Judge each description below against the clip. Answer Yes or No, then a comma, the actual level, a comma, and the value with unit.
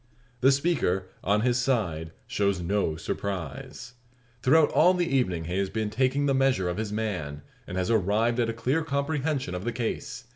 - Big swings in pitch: Yes, wide, 6.3 semitones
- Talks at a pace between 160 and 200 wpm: Yes, average, 180 wpm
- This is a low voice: Yes, low, 110 Hz